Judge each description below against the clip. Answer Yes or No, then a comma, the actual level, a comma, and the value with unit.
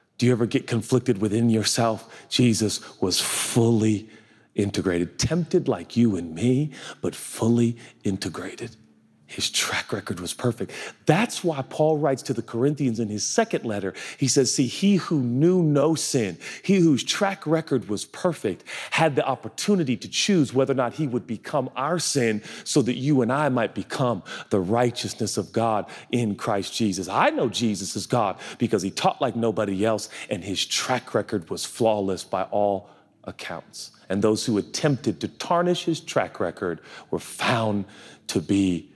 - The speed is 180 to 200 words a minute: No, average, 170 wpm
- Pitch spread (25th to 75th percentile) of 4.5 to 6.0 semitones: Yes, average, 5.1 semitones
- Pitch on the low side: Yes, low, 120 Hz